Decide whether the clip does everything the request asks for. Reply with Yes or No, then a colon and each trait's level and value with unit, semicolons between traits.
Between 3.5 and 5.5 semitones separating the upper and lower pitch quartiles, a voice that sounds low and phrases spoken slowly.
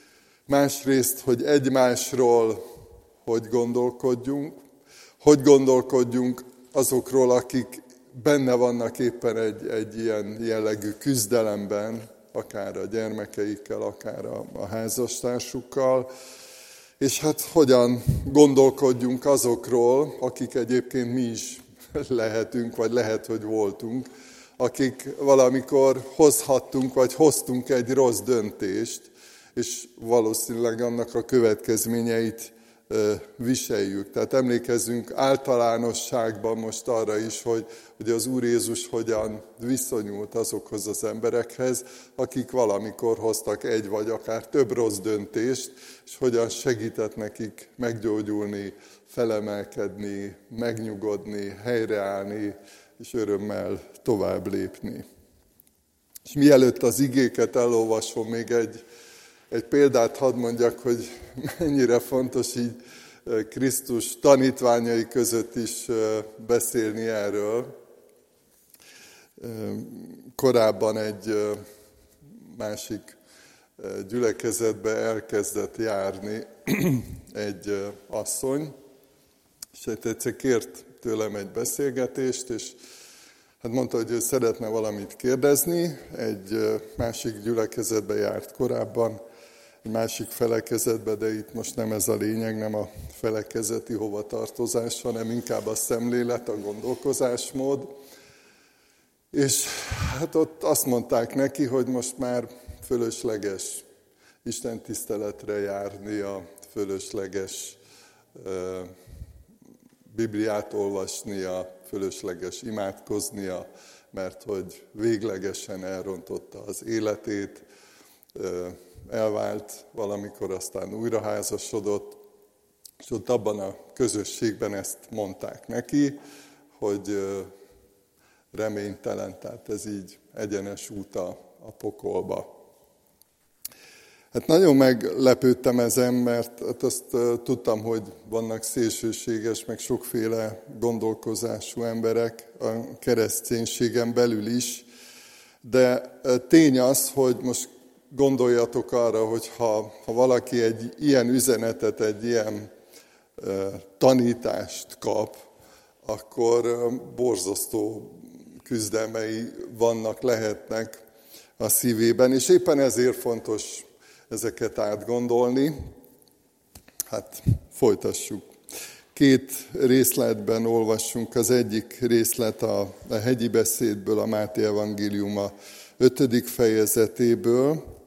No: average, 2.8 semitones; low, 115 Hz; slow, 95 wpm